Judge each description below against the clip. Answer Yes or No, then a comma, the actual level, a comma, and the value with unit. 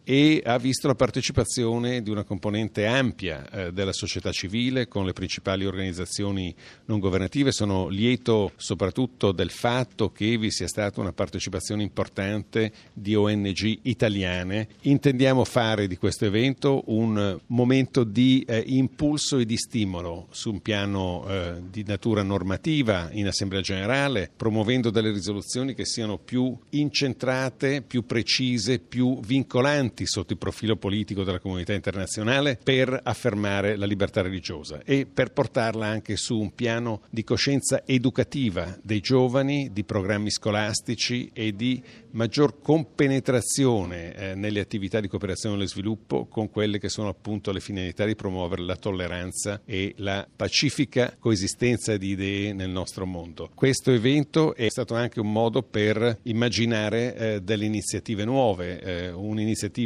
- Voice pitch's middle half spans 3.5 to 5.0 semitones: Yes, average, 4.0 semitones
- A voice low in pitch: Yes, low, 110 Hz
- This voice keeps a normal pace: Yes, average, 140 wpm